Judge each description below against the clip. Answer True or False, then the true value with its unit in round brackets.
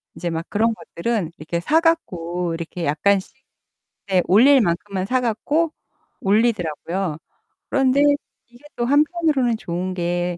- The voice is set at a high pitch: True (195 Hz)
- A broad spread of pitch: True (6.6 semitones)